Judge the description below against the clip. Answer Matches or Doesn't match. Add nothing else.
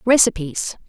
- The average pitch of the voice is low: Doesn't match